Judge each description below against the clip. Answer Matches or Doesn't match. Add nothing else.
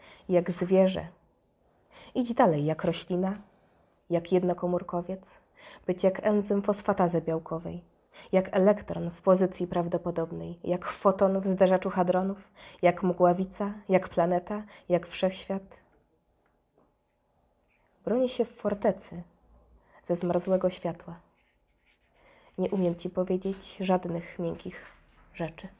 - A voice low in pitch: Doesn't match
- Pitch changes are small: Matches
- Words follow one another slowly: Matches